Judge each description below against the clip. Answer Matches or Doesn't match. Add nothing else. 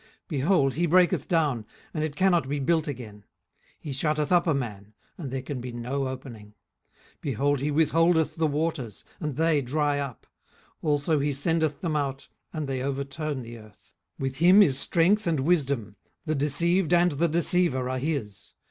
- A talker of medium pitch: Matches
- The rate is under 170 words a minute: Doesn't match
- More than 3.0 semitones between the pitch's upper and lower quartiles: Matches